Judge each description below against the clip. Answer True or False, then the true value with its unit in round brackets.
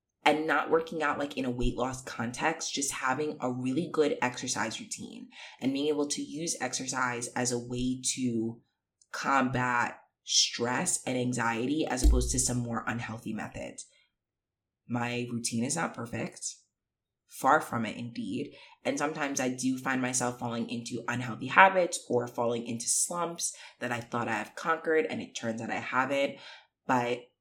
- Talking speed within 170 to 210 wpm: False (160 wpm)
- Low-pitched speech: True (125 Hz)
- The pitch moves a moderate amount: True (3.1 semitones)